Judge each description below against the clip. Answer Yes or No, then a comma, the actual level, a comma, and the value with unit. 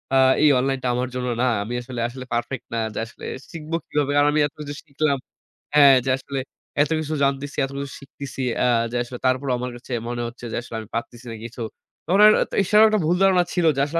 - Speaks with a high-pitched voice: No, low, 135 Hz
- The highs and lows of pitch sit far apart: No, average, 3.3 semitones